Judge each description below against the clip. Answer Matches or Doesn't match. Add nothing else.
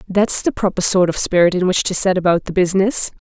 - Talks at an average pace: Doesn't match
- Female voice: Matches